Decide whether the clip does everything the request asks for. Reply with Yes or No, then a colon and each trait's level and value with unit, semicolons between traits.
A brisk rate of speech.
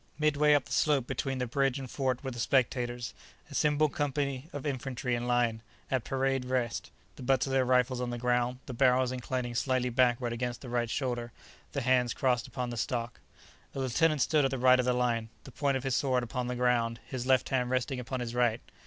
Yes: fast, 215 wpm